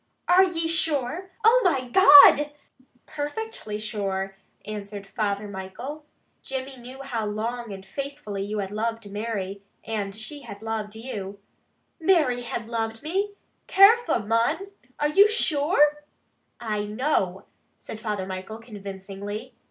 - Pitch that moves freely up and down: Yes, wide, 6.3 semitones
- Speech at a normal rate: No, slow, 130 wpm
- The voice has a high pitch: Yes, high, 230 Hz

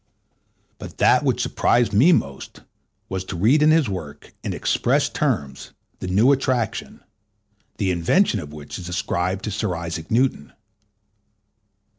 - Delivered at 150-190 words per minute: No, average, 140 wpm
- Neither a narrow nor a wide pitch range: No, wide, 6.3 semitones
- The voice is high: No, very low, 95 Hz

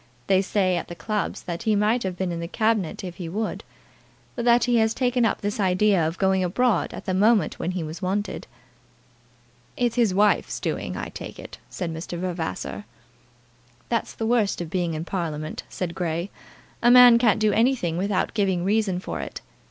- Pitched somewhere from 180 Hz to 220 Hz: Yes, high, 190 Hz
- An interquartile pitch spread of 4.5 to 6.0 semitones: No, average, 4.1 semitones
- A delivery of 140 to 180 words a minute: No, average, 195 wpm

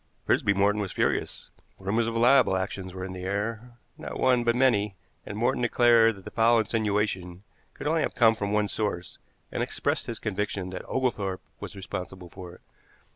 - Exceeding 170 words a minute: Yes, average, 180 wpm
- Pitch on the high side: No, low, 105 Hz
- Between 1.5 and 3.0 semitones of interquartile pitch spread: No, average, 3.6 semitones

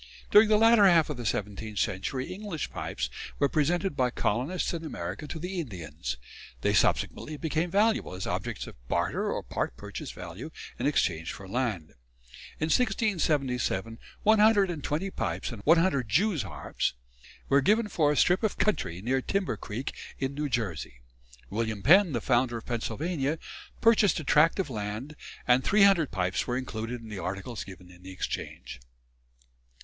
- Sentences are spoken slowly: No, average, 165 wpm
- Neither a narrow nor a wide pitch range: No, wide, 8.9 semitones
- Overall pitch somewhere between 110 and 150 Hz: Yes, low, 135 Hz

